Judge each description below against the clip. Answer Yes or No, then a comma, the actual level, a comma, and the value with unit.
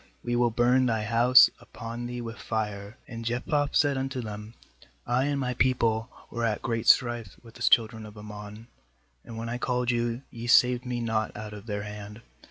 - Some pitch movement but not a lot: No, narrow, 2.2 semitones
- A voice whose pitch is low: Yes, low, 115 Hz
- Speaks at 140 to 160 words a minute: No, average, 190 wpm